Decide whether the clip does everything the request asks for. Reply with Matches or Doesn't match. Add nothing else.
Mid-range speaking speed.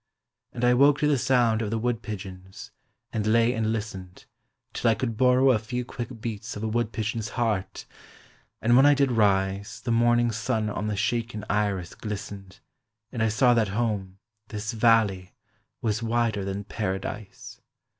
Matches